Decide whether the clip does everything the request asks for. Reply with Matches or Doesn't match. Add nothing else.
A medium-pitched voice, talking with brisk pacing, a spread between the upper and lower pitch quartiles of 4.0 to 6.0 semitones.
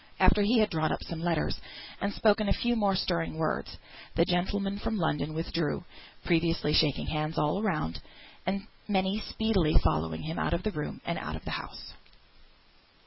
Doesn't match